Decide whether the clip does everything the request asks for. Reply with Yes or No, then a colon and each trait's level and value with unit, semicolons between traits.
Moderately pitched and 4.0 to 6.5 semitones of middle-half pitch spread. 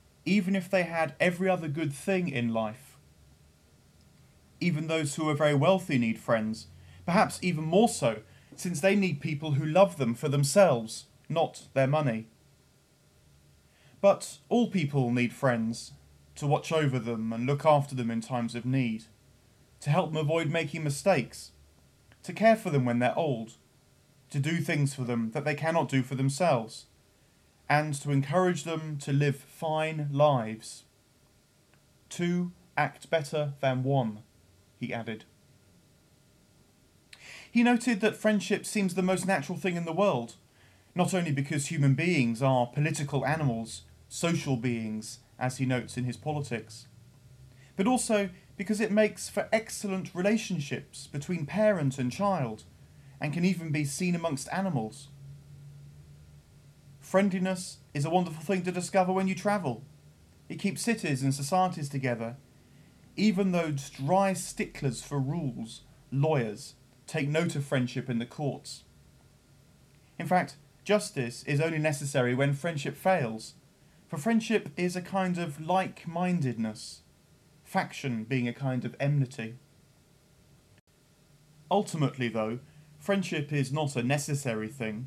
Yes: medium, 145 Hz; wide, 5.6 semitones